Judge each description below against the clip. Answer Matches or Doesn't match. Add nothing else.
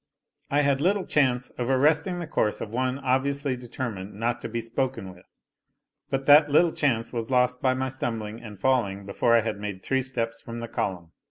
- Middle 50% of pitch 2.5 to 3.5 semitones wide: Matches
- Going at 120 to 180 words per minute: Doesn't match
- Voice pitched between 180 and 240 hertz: Doesn't match